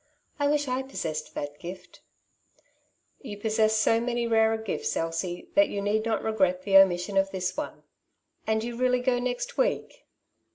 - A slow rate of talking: No, average, 165 wpm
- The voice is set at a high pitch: Yes, high, 220 Hz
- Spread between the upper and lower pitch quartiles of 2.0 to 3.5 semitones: No, average, 4.3 semitones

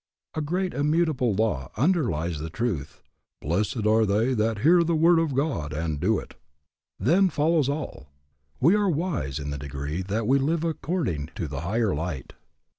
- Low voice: Yes, low, 115 Hz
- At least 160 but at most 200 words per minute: Yes, average, 170 wpm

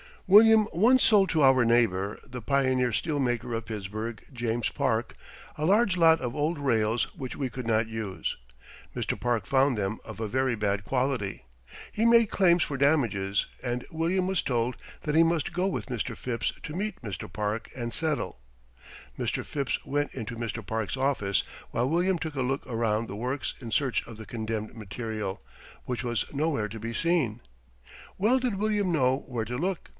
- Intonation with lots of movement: Yes, wide, 6.2 semitones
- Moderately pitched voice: No, low, 125 Hz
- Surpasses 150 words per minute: Yes, average, 180 wpm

